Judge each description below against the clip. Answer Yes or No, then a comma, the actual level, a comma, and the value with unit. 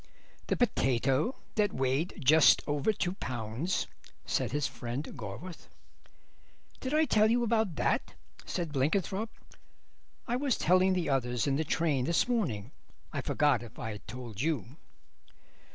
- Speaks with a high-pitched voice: No, medium, 150 Hz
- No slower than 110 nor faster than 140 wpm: Yes, slow, 135 wpm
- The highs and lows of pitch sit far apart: Yes, wide, 7.4 semitones